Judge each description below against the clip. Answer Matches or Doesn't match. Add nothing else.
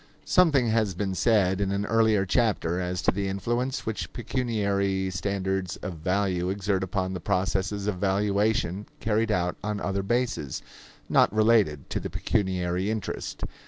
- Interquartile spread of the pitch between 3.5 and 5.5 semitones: Doesn't match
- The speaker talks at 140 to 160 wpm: Matches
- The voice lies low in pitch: Matches